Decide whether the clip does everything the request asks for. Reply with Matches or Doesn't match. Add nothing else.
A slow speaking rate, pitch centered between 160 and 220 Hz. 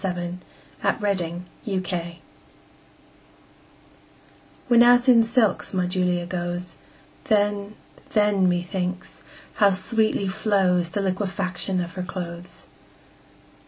Matches